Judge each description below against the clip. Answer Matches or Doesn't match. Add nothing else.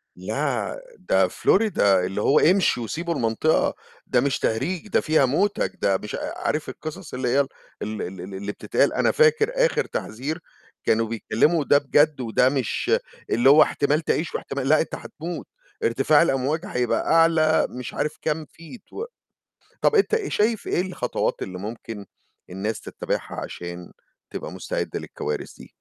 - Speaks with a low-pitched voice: Doesn't match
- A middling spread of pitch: Doesn't match